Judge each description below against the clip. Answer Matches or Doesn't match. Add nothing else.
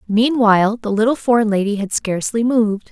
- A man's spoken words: Doesn't match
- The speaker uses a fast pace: Doesn't match